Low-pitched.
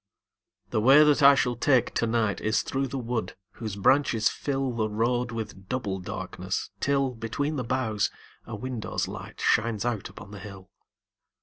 Yes: low, 115 Hz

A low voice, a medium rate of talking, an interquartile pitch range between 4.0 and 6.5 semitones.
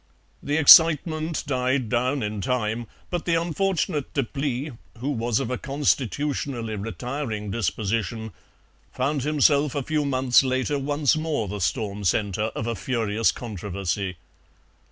No: low, 125 Hz; slow, 130 wpm; average, 4.8 semitones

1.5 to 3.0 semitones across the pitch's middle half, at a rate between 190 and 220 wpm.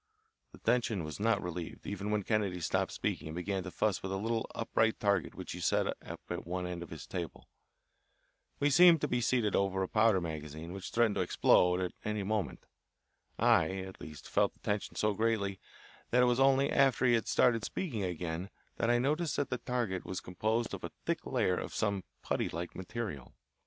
No: average, 4.4 semitones; fast, 205 wpm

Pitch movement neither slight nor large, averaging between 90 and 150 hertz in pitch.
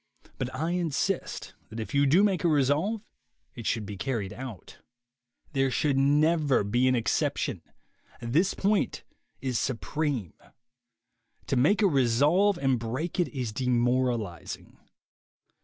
Yes: average, 5.0 semitones; low, 135 Hz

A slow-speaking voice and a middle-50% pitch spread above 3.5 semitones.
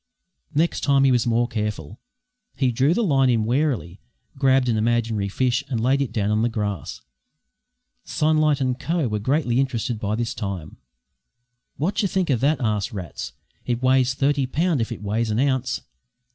No: average, 175 wpm; average, 4.1 semitones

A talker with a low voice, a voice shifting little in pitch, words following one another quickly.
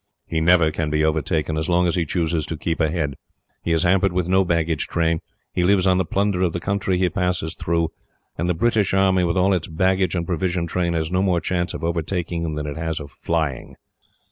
Yes: very low, 85 Hz; narrow, 2.2 semitones; fast, 225 wpm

